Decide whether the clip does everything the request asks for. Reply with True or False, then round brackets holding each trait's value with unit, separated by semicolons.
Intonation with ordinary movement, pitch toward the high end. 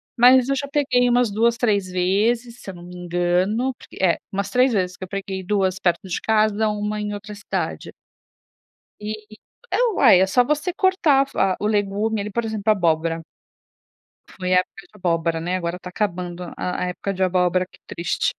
True (4.0 semitones; 200 Hz)